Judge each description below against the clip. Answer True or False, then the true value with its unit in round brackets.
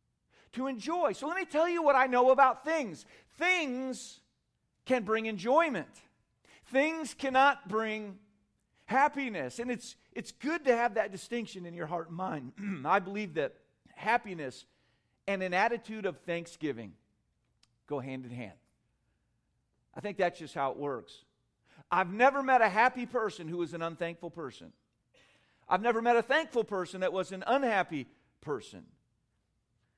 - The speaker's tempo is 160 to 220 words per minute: False (150 wpm)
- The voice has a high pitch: True (205 Hz)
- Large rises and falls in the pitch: True (8.4 semitones)